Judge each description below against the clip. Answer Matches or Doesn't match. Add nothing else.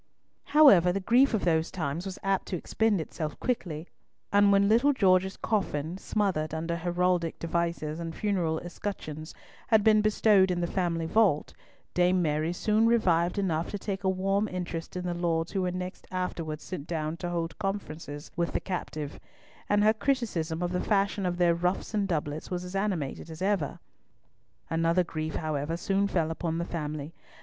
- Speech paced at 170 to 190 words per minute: Matches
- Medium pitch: Matches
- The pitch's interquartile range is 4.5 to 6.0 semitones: Doesn't match